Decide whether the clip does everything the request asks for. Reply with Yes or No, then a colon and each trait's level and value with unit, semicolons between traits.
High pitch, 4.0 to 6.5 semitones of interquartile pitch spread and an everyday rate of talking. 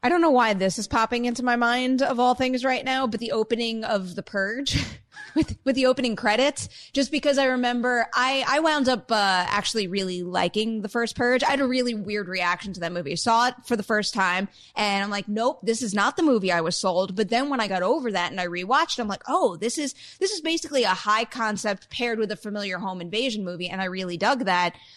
No: high, 225 Hz; average, 4.4 semitones; fast, 245 wpm